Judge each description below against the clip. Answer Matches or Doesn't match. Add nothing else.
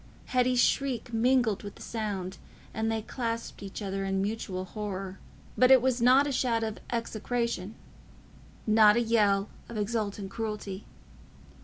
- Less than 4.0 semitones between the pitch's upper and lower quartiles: Matches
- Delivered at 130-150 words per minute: Matches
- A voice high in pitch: Matches